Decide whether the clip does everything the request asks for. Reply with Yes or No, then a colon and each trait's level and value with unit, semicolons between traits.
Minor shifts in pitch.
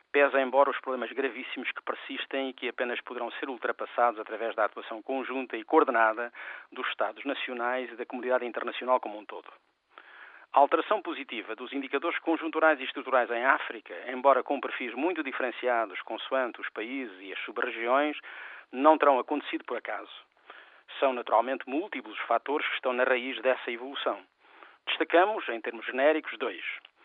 Yes: narrow, 2.3 semitones